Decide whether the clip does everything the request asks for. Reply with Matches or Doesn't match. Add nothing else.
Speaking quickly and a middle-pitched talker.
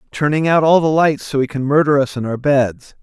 Matches